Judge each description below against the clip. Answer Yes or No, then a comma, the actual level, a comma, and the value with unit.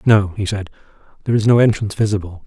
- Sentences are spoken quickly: No, average, 195 wpm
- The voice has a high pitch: No, low, 105 Hz